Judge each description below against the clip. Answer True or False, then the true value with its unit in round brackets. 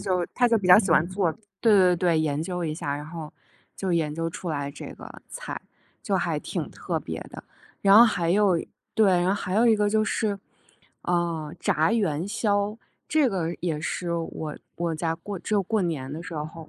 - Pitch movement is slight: False (4.0 semitones)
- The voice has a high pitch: False (175 Hz)